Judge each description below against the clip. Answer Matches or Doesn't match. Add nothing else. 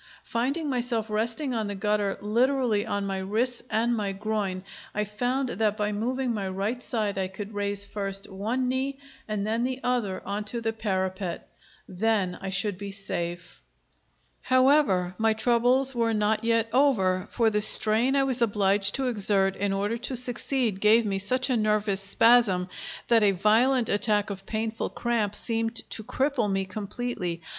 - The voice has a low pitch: Doesn't match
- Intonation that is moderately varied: Matches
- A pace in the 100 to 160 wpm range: Doesn't match